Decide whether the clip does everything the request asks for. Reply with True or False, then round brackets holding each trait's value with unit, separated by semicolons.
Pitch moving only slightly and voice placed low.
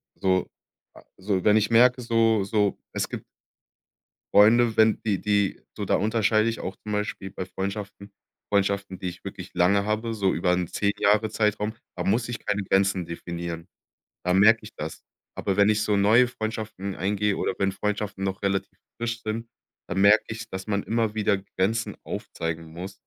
True (2.3 semitones; 100 Hz)